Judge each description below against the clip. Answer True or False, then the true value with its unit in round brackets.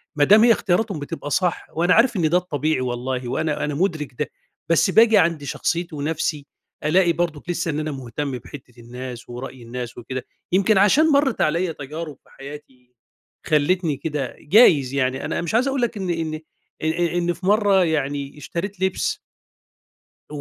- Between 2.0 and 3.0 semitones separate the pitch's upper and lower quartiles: False (4.5 semitones)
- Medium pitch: True (155 Hz)